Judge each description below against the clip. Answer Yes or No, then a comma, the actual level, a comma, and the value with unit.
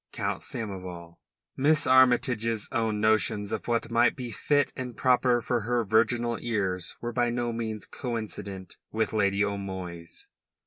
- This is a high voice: No, low, 115 Hz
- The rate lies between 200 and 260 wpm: No, average, 140 wpm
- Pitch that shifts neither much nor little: Yes, average, 3.2 semitones